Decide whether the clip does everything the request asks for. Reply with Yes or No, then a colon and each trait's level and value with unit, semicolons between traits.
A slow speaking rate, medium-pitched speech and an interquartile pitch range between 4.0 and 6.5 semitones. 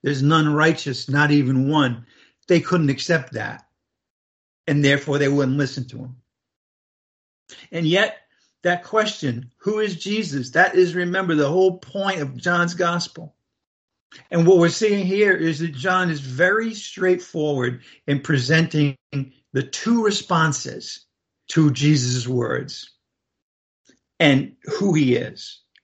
Yes: slow, 130 wpm; medium, 150 Hz; average, 5.2 semitones